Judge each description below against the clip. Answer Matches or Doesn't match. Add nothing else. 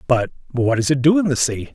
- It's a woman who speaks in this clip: Doesn't match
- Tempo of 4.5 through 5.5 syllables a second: Doesn't match